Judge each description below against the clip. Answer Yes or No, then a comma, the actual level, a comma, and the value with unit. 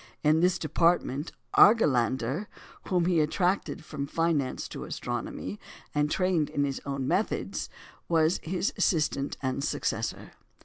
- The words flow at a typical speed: No, slow, 125 wpm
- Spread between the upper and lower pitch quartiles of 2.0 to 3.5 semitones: No, average, 4.0 semitones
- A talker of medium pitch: Yes, medium, 155 Hz